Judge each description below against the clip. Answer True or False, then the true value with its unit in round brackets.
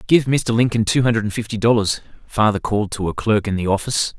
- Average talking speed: False (230 wpm)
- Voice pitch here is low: True (110 Hz)